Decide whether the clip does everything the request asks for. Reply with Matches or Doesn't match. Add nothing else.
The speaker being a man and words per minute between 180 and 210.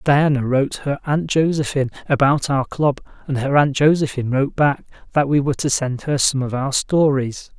Matches